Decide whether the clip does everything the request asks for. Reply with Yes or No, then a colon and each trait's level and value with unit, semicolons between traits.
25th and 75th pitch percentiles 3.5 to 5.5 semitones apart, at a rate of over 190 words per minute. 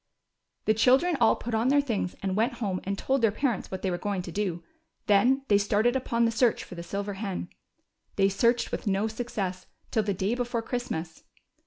Yes: average, 3.9 semitones; fast, 205 wpm